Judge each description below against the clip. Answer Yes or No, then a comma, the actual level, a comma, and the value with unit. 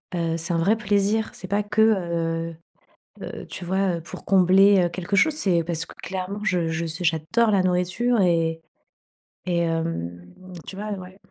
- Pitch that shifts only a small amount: No, average, 3.2 semitones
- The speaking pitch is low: No, medium, 180 Hz